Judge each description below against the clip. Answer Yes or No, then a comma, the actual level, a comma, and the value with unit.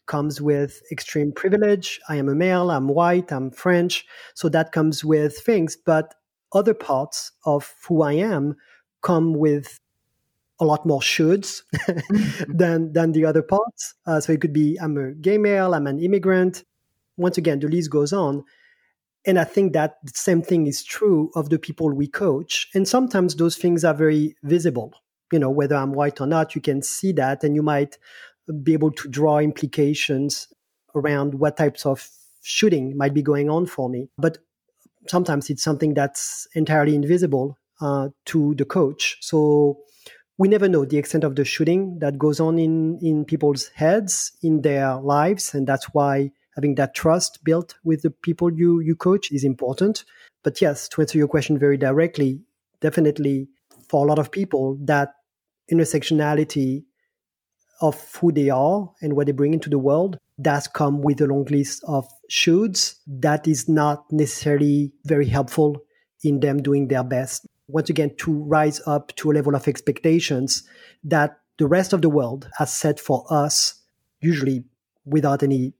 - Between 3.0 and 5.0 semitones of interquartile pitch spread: No, narrow, 2.6 semitones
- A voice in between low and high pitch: Yes, medium, 150 Hz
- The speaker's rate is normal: Yes, average, 175 wpm